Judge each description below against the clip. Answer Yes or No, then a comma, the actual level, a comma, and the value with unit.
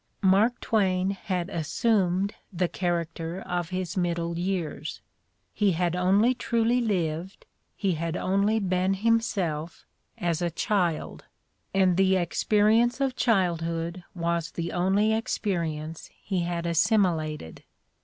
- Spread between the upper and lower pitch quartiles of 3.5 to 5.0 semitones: No, average, 3.1 semitones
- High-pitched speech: No, medium, 180 Hz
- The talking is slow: Yes, slow, 120 wpm